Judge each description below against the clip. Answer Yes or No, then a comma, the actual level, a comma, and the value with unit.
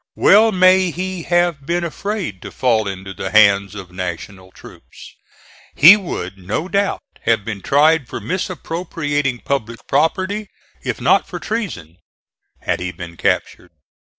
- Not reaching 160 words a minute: Yes, average, 140 wpm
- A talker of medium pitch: Yes, medium, 145 Hz